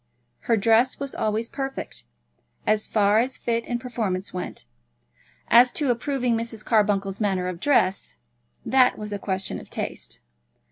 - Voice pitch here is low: No, high, 225 Hz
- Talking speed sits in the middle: Yes, average, 145 wpm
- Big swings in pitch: No, average, 3.8 semitones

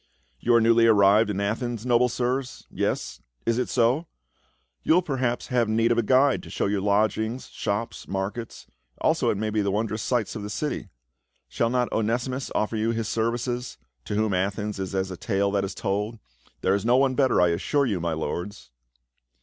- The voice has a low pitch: Yes, low, 110 Hz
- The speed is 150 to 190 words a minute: No, fast, 205 wpm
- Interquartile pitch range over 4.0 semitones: No, average, 3.3 semitones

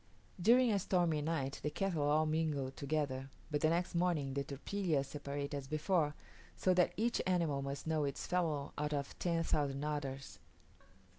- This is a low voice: No, medium, 150 Hz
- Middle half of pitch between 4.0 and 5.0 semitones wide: No, average, 3.5 semitones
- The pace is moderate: Yes, average, 165 wpm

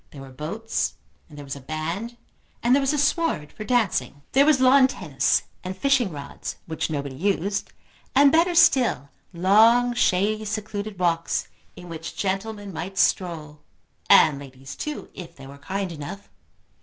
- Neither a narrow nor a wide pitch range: No, wide, 7.6 semitones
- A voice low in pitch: No, high, 195 Hz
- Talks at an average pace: Yes, average, 160 wpm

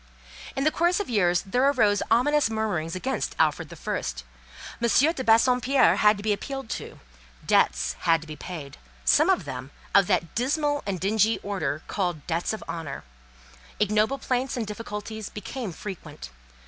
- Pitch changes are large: Yes, wide, 6.2 semitones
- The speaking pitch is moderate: No, high, 210 Hz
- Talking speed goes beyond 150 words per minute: Yes, average, 160 wpm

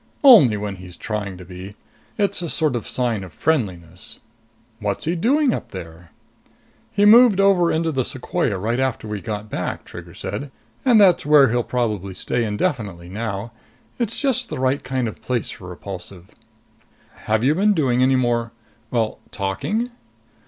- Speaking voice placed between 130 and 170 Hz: No, low, 120 Hz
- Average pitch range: No, wide, 8.4 semitones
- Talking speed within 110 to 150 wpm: No, average, 165 wpm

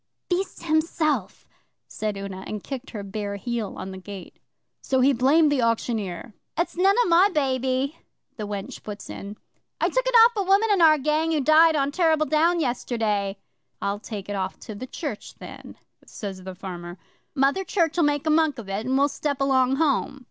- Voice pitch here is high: Yes, very high, 265 Hz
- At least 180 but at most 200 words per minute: Yes, average, 190 wpm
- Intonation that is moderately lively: No, wide, 7.3 semitones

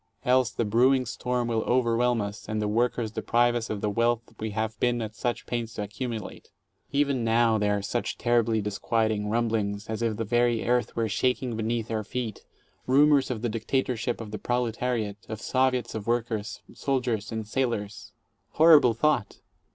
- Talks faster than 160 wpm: Yes, average, 175 wpm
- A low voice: Yes, low, 115 Hz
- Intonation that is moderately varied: No, narrow, 2.1 semitones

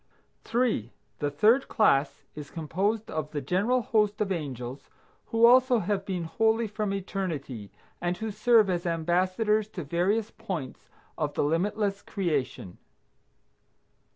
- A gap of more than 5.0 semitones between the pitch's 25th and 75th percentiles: Yes, wide, 5.6 semitones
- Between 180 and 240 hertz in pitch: Yes, high, 190 Hz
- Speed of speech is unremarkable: No, slow, 130 wpm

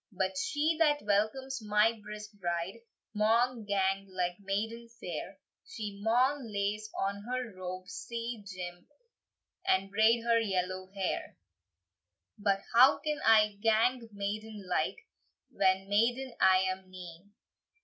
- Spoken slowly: Yes, slow, 125 wpm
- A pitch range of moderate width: Yes, average, 3.3 semitones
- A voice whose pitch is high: Yes, high, 210 Hz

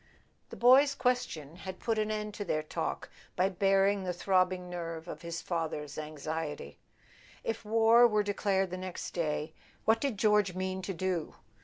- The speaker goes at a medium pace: Yes, average, 165 wpm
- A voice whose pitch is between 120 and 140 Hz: No, medium, 185 Hz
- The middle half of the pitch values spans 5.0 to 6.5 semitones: No, average, 4.1 semitones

